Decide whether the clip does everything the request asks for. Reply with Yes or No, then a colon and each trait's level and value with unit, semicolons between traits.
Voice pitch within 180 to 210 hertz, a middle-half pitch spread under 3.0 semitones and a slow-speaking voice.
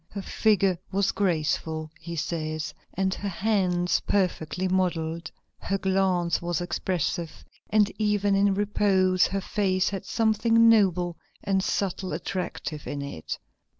Yes: medium, 185 Hz; narrow, 2.6 semitones; slow, 125 wpm